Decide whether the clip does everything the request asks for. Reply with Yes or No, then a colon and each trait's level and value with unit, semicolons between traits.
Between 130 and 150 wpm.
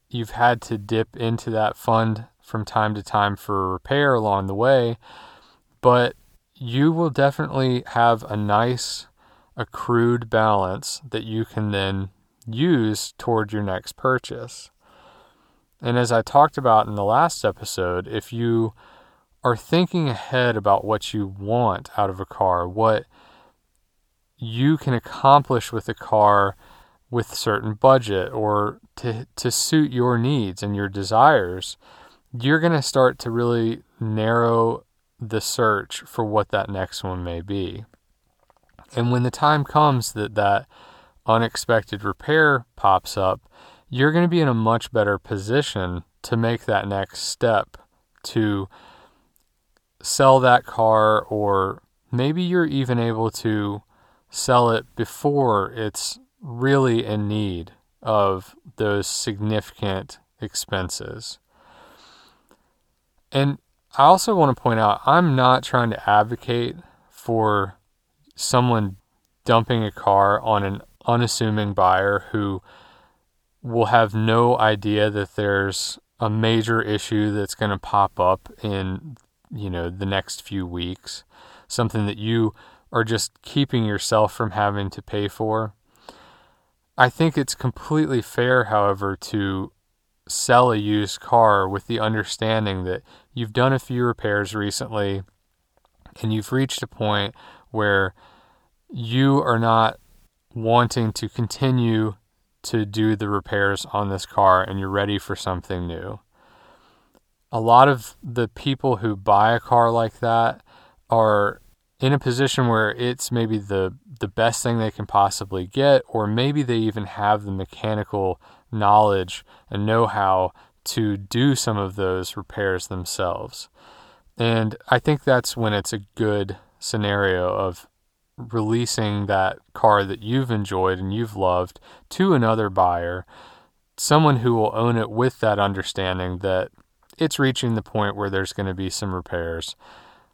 Yes: average, 140 wpm